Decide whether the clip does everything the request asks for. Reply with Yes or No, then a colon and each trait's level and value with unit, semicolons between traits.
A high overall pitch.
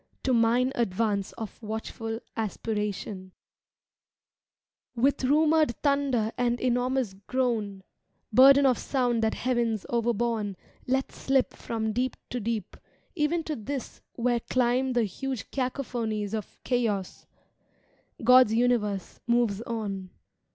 Yes: high, 235 Hz